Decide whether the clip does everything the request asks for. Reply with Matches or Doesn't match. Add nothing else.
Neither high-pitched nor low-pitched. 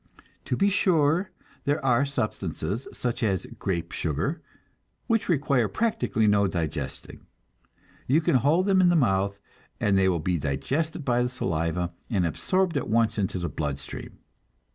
Doesn't match